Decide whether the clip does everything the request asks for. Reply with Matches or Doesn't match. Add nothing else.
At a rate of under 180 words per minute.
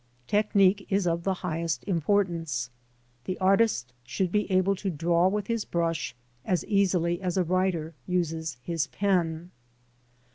Matches